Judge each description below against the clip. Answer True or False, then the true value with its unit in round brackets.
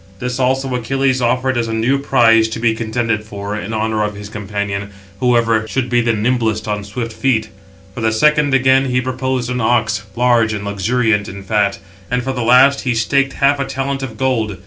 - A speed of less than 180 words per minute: False (200 wpm)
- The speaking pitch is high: False (115 Hz)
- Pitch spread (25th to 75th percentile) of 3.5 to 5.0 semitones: False (2.9 semitones)